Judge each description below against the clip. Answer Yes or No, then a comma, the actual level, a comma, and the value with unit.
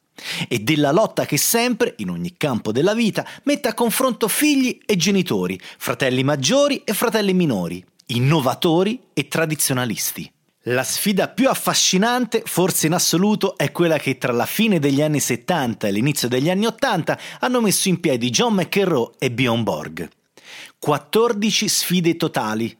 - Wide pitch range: Yes, wide, 8.1 semitones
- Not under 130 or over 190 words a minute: Yes, average, 150 wpm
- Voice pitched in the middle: Yes, medium, 170 Hz